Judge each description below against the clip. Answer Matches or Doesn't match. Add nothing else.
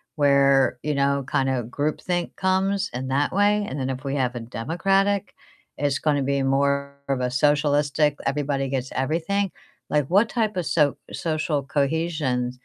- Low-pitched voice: Doesn't match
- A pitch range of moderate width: Matches